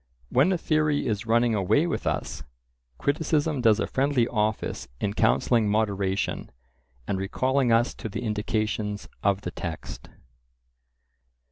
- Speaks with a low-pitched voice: Yes, low, 110 Hz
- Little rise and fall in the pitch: No, average, 4.5 semitones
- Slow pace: Yes, slow, 130 wpm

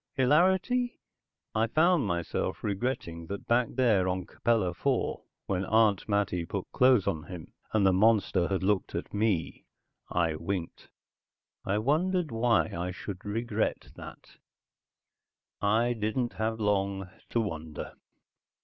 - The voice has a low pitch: Yes, low, 105 Hz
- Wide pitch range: No, average, 4.2 semitones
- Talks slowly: Yes, slow, 130 wpm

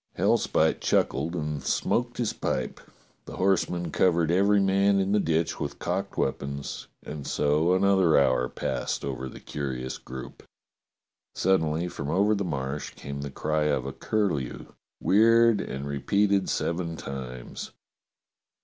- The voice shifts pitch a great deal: Yes, wide, 5.7 semitones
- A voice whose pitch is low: Yes, very low, 80 Hz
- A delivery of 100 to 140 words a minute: Yes, slow, 135 wpm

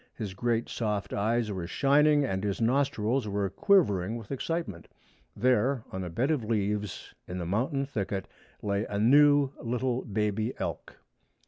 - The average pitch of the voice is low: Yes, low, 110 Hz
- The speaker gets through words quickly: No, average, 150 wpm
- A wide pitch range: No, average, 5.0 semitones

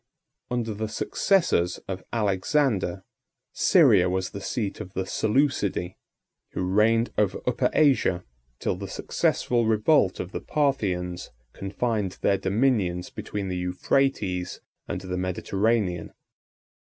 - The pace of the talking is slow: Yes, slow, 120 wpm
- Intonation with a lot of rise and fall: No, average, 4.1 semitones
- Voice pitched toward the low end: Yes, low, 100 Hz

